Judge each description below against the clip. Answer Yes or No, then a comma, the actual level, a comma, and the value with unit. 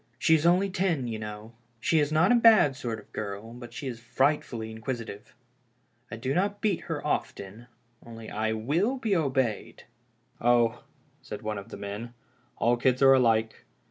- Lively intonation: Yes, wide, 5.7 semitones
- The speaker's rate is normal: Yes, average, 185 wpm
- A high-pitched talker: No, low, 120 Hz